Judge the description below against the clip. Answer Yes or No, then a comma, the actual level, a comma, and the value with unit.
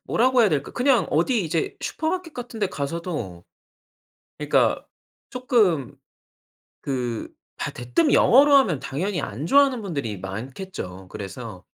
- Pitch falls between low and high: Yes, medium, 165 Hz